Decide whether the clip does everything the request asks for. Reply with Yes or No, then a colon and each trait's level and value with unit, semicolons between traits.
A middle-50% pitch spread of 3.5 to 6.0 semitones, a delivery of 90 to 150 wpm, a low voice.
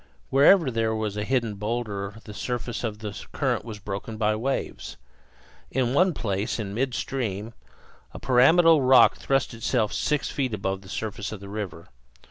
No: average, 3.8 semitones; average, 160 wpm; low, 110 Hz